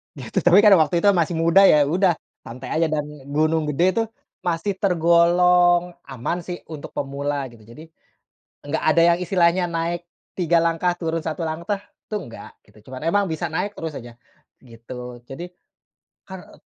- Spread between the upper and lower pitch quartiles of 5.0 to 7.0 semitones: No, average, 3.5 semitones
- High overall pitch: No, medium, 165 Hz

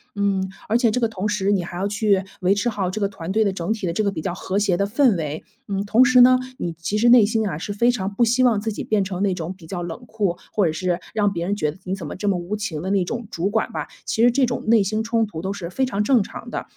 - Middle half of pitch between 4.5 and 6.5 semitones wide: No, average, 3.3 semitones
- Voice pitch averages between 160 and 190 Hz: No, high, 200 Hz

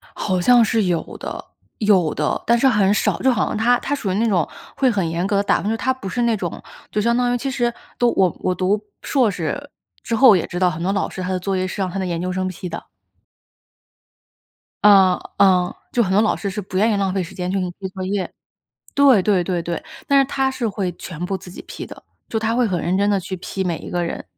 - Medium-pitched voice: No, high, 195 Hz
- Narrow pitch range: No, average, 3.9 semitones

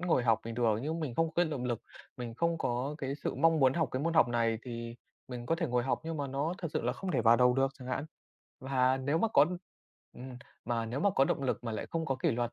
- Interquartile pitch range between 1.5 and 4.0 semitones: No, average, 4.7 semitones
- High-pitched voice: No, low, 130 Hz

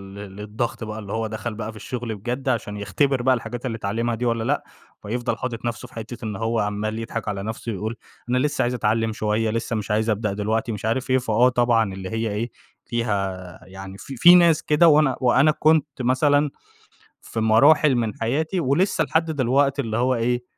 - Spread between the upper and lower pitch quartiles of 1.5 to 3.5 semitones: Yes, average, 3.1 semitones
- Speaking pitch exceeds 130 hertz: No, low, 115 Hz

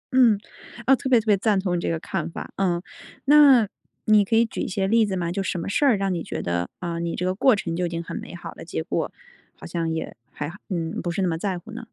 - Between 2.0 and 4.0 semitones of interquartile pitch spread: No, average, 4.5 semitones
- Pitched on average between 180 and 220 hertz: Yes, high, 190 Hz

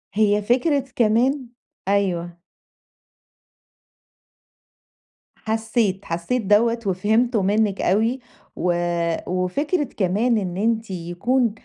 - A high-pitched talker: Yes, high, 215 Hz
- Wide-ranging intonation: No, average, 4.0 semitones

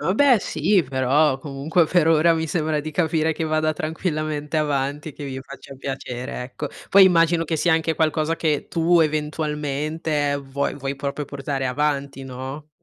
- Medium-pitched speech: Yes, medium, 150 Hz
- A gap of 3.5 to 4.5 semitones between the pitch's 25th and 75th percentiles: No, narrow, 2.5 semitones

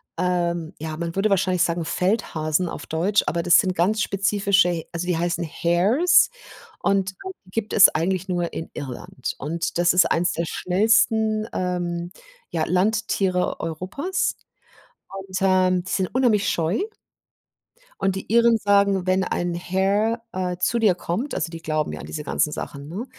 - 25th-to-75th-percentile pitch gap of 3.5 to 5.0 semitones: No, average, 2.8 semitones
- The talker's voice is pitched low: No, medium, 185 Hz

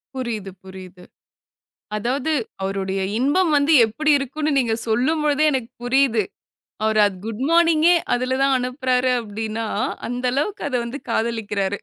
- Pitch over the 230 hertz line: Yes, very high, 250 Hz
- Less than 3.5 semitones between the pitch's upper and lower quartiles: No, average, 4.6 semitones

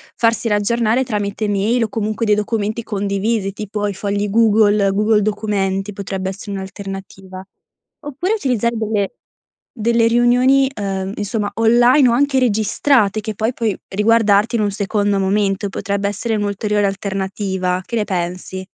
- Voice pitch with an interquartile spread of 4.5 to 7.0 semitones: No, narrow, 2.5 semitones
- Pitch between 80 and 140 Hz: No, high, 210 Hz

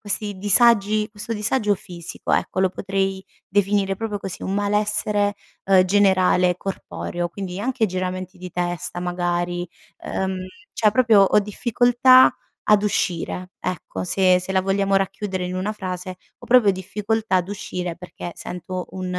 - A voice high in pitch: Yes, high, 195 Hz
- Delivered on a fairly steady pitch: Yes, narrow, 2.3 semitones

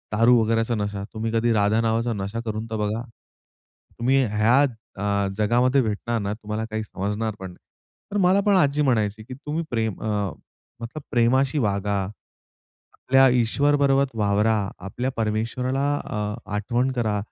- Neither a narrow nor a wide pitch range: Yes, average, 3.3 semitones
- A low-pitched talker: Yes, low, 115 Hz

